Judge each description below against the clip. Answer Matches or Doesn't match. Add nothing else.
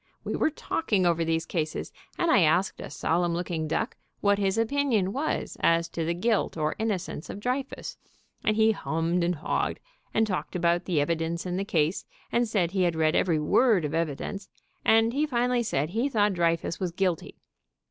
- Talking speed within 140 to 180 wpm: Doesn't match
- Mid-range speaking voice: Matches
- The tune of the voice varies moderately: Matches